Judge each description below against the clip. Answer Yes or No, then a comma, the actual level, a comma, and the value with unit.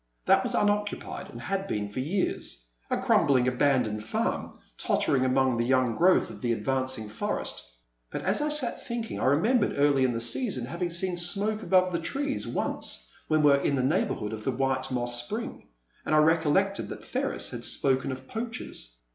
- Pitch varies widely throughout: Yes, wide, 7.0 semitones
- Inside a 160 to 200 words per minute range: Yes, average, 190 wpm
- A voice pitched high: No, medium, 140 Hz